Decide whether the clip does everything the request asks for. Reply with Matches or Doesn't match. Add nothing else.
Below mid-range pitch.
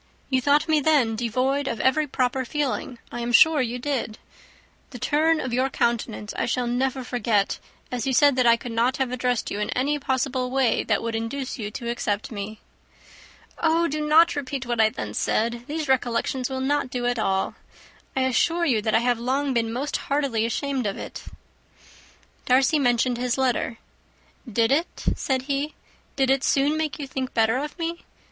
Doesn't match